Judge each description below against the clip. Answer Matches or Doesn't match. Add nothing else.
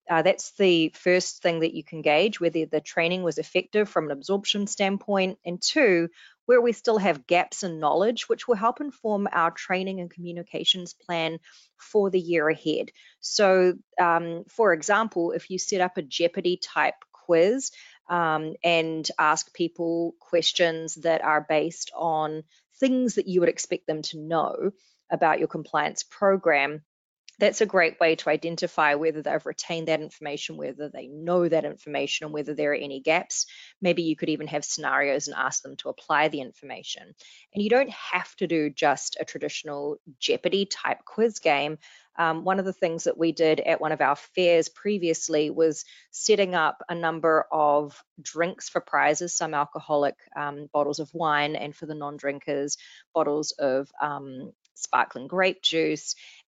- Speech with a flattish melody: Doesn't match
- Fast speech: Doesn't match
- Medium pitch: Matches